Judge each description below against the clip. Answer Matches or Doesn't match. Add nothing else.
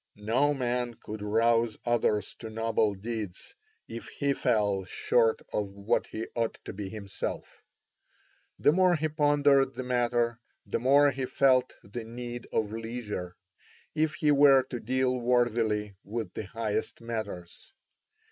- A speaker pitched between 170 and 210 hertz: Doesn't match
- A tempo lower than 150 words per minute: Matches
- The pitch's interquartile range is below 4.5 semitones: Matches